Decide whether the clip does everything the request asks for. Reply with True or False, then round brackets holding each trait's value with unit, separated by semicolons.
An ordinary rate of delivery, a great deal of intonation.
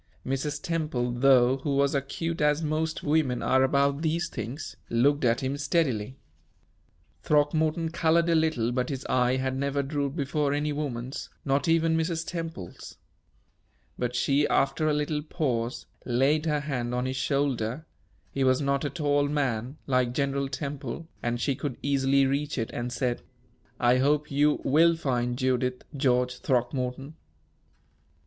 False (150 wpm; 2.9 semitones)